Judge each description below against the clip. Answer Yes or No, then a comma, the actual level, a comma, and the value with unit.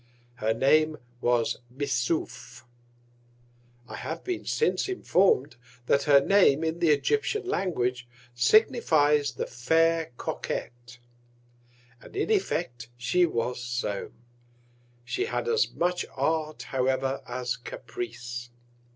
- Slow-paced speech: Yes, slow, 110 wpm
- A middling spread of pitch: No, wide, 6.5 semitones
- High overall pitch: No, medium, 145 Hz